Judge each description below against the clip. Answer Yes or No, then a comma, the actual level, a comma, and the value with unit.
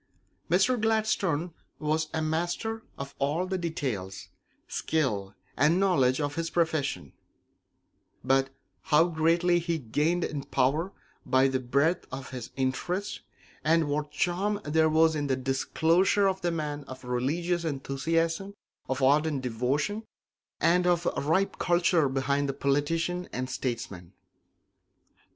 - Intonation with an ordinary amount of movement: Yes, average, 4.4 semitones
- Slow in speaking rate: Yes, slow, 130 wpm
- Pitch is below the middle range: No, medium, 155 Hz